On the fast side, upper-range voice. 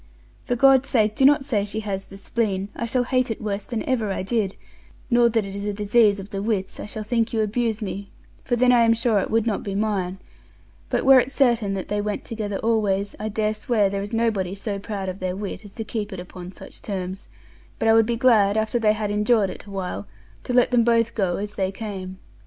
Yes: fast, 240 wpm; high, 210 Hz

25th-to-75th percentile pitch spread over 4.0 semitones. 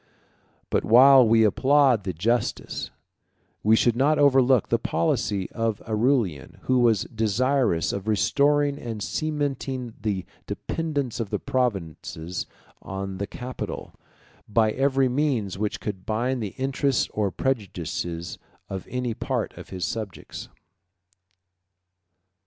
Yes: average, 4.9 semitones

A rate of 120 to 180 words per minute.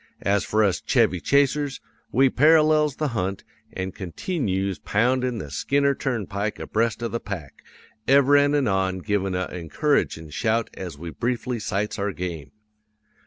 Yes: average, 145 wpm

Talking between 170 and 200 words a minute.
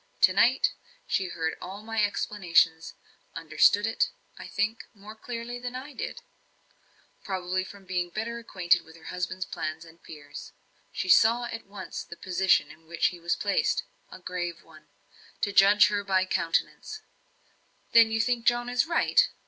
No: average, 160 wpm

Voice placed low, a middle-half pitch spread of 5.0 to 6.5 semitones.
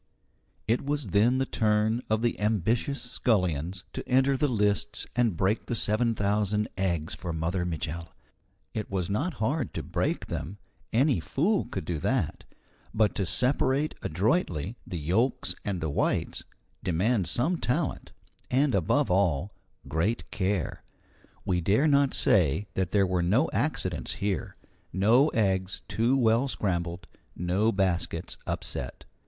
Yes: low, 105 Hz; average, 5.3 semitones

